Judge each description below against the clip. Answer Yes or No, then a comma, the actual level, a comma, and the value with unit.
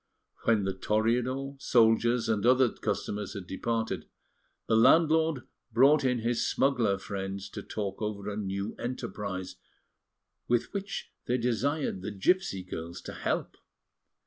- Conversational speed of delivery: No, slow, 130 wpm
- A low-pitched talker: Yes, low, 115 Hz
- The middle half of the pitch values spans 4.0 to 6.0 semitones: Yes, average, 4.3 semitones